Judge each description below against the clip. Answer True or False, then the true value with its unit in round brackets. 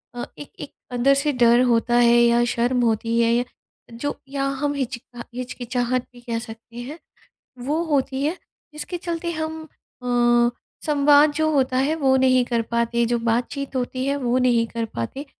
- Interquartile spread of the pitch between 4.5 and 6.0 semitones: False (3.2 semitones)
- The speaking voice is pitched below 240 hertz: False (255 Hz)